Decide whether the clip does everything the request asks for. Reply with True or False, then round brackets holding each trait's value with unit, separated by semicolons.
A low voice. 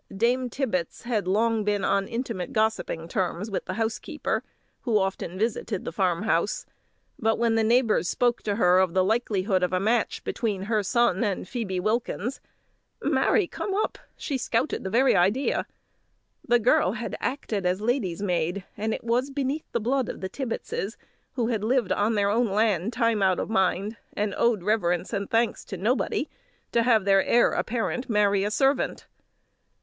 False (220 Hz)